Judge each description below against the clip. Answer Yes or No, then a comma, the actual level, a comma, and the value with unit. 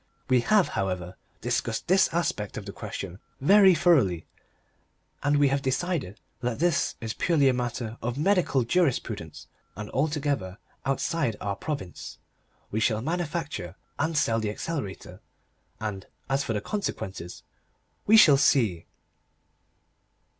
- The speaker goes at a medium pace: No, slow, 130 wpm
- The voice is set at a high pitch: No, low, 130 Hz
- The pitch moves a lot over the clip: Yes, wide, 7.3 semitones